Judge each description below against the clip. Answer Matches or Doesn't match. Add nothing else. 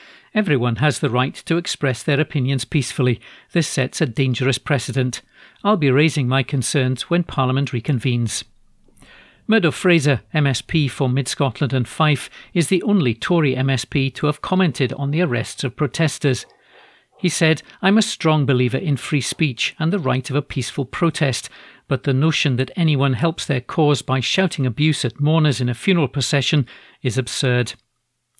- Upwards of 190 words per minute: Doesn't match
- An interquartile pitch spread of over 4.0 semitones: Doesn't match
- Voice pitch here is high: Doesn't match